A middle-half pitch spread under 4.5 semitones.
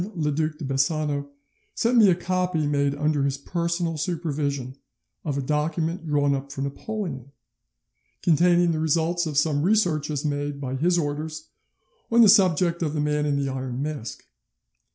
Yes: average, 3.1 semitones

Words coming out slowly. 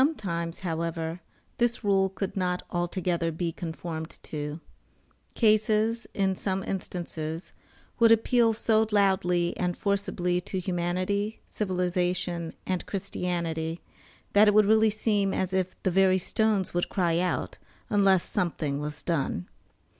Yes: slow, 125 wpm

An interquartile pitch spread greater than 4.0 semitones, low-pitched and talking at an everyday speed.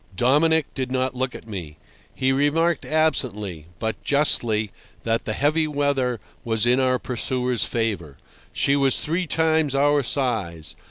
Yes: average, 4.5 semitones; low, 130 Hz; average, 145 wpm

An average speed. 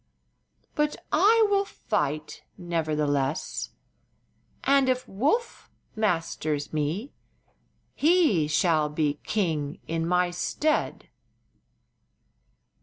No: slow, 80 wpm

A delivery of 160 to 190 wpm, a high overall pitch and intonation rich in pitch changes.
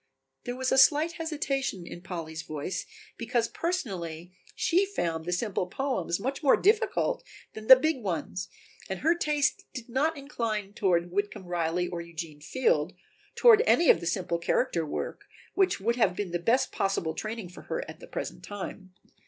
Yes: average, 170 wpm; high, 205 Hz; wide, 7.7 semitones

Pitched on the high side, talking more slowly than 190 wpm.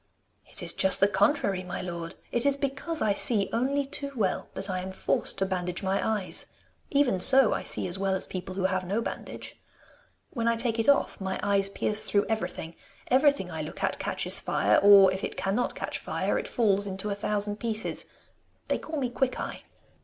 No: high, 200 Hz; average, 200 wpm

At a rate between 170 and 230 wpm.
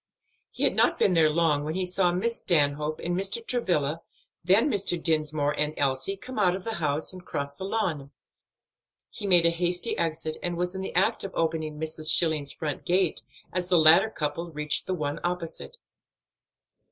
Yes: average, 185 wpm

